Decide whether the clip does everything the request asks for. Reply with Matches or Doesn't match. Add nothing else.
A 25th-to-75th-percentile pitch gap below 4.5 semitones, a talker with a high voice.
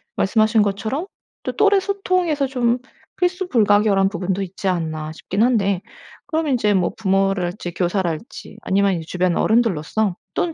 Doesn't match